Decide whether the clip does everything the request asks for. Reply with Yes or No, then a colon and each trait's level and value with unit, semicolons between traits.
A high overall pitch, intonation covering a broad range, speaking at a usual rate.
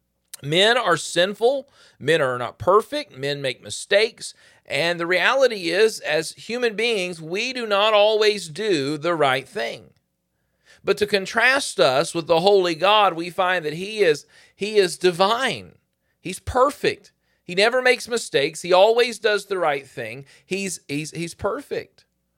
Yes: high, 195 Hz; wide, 5.7 semitones; average, 155 wpm